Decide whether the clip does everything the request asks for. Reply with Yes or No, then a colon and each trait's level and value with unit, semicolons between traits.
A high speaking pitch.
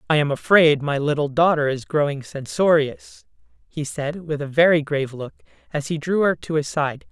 No: medium, 150 Hz